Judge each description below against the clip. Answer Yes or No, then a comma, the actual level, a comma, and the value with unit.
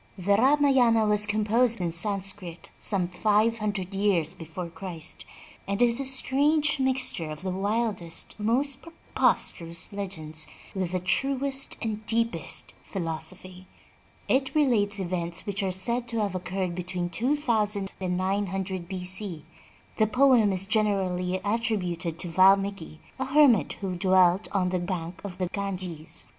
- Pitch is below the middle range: No, high, 195 Hz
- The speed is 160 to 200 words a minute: No, average, 150 wpm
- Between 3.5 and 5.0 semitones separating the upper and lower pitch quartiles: Yes, average, 4.1 semitones